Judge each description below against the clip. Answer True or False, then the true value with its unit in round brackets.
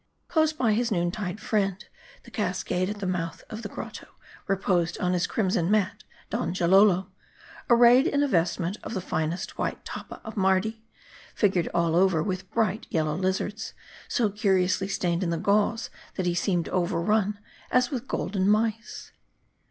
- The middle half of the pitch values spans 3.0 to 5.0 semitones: True (3.4 semitones)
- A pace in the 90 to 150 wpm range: False (165 wpm)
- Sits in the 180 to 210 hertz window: True (190 Hz)